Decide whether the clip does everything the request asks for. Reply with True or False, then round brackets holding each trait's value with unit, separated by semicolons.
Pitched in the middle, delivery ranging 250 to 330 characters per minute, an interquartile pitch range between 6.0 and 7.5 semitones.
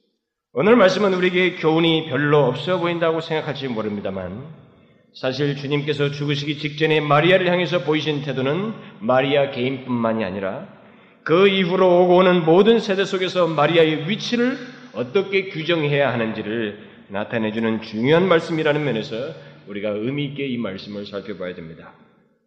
False (150 Hz; 355 characters per minute; 6.7 semitones)